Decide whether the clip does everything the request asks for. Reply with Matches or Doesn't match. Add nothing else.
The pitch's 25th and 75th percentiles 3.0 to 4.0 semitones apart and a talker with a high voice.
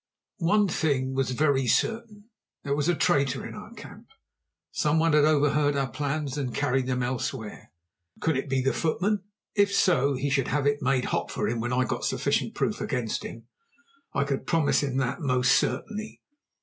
Doesn't match